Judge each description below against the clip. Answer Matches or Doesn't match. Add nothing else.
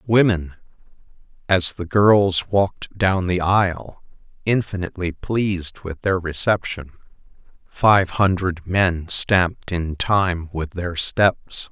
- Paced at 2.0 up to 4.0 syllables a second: Matches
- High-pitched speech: Doesn't match